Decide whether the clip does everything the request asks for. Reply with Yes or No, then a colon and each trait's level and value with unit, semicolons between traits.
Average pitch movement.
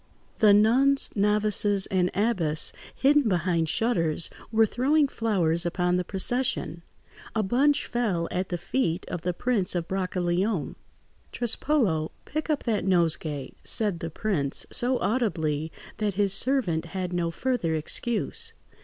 No: wide, 5.8 semitones